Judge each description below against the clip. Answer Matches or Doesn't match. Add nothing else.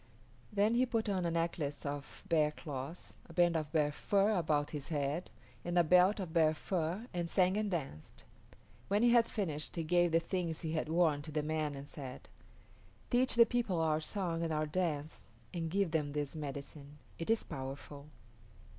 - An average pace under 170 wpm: Doesn't match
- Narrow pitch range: Doesn't match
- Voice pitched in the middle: Matches